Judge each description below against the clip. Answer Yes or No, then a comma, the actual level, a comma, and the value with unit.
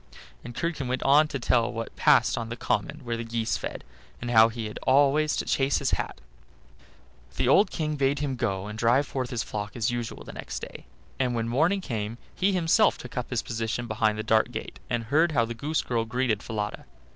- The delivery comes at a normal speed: No, fast, 215 wpm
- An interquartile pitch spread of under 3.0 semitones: No, average, 3.7 semitones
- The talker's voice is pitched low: Yes, low, 120 Hz